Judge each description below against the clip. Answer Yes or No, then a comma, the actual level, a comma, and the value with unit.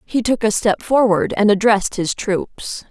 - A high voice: Yes, high, 210 Hz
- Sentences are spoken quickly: No, average, 185 wpm